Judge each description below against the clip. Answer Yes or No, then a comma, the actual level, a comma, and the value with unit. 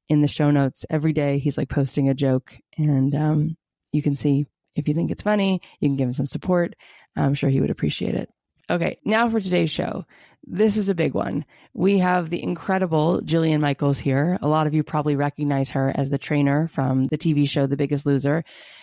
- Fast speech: Yes, fast, 215 wpm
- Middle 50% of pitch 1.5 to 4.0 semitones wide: Yes, average, 2.9 semitones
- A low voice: No, medium, 150 Hz